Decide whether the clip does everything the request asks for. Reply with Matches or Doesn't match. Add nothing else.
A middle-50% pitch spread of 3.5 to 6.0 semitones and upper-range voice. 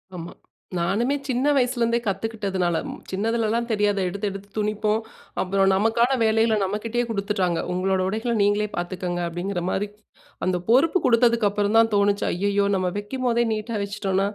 Doesn't match